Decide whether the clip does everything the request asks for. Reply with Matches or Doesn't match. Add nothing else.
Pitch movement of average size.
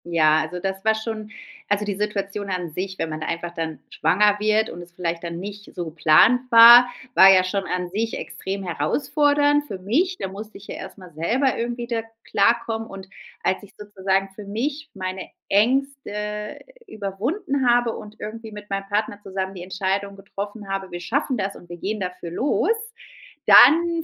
Matches